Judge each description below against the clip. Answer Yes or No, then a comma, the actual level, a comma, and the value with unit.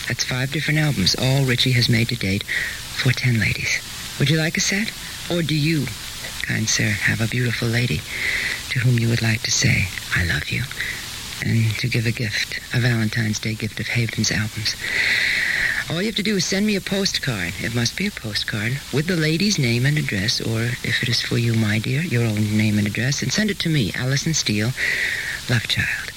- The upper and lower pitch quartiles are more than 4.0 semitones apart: Yes, average, 5.2 semitones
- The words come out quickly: Yes, fast, 210 wpm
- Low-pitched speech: Yes, low, 120 Hz